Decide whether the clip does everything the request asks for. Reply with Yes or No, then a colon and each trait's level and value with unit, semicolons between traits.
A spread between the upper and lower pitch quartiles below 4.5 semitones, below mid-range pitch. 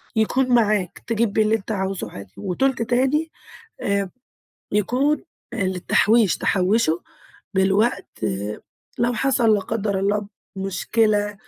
No: average, 3.2 semitones; high, 210 Hz